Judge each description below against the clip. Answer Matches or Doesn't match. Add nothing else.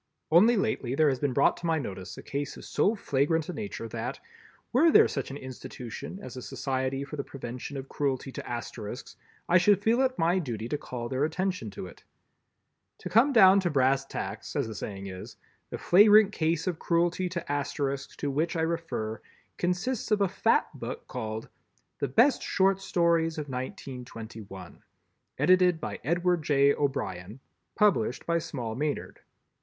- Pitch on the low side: Doesn't match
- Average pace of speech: Matches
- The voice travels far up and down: Matches